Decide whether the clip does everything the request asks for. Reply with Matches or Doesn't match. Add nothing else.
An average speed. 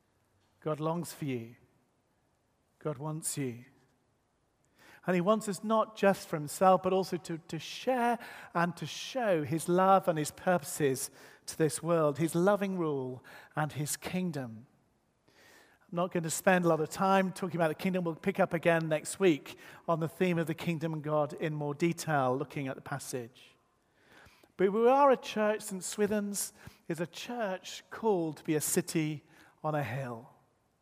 Matches